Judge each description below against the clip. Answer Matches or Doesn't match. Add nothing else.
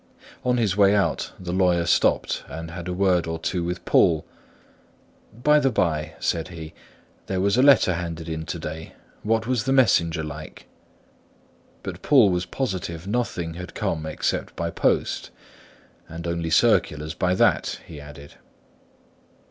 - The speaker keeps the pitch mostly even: Doesn't match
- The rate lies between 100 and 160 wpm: Matches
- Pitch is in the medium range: Doesn't match